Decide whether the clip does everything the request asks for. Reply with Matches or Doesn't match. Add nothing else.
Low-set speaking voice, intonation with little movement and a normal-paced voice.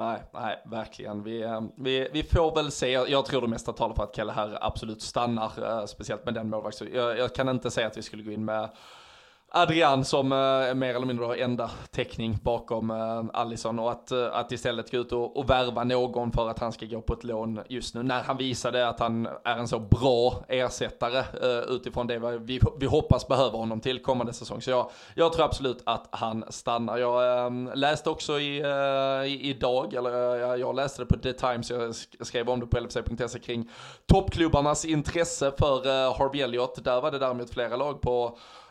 Doesn't match